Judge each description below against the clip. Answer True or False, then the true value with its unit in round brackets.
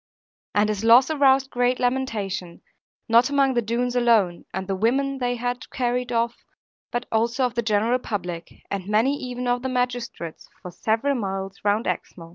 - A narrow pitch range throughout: False (3.3 semitones)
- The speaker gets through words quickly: False (170 wpm)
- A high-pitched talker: True (235 Hz)